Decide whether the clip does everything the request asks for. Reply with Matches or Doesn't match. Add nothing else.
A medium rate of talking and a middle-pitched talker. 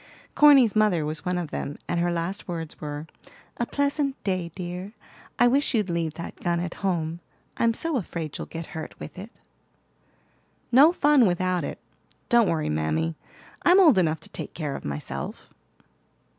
Matches